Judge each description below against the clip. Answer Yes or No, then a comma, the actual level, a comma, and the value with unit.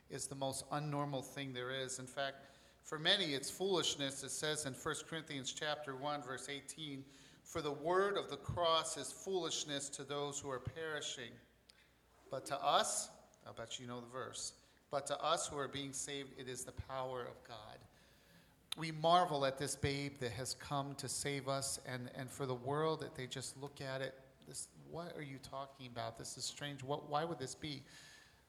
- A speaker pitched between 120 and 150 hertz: Yes, medium, 140 Hz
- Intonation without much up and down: Yes, narrow, 2.0 semitones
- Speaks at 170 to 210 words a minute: Yes, average, 195 wpm